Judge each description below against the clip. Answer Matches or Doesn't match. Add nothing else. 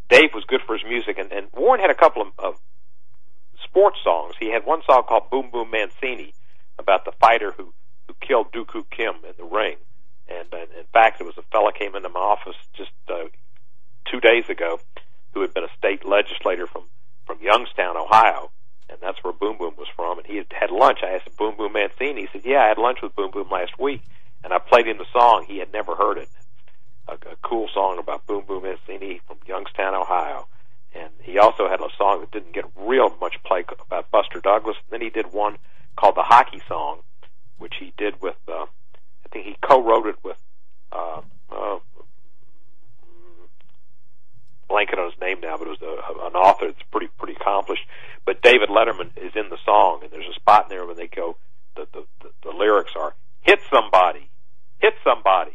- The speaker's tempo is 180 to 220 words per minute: Matches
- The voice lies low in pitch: Doesn't match